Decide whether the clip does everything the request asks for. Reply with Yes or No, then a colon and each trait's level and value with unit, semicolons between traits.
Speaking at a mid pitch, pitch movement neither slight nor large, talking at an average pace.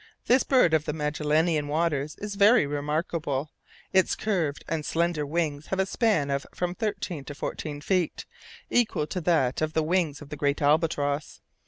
Yes: medium, 155 Hz; average, 3.4 semitones; average, 170 wpm